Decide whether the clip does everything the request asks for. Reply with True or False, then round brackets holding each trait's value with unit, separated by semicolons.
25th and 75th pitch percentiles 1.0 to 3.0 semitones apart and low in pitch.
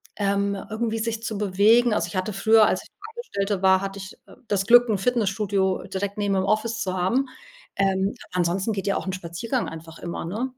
False (2.7 semitones; 200 Hz)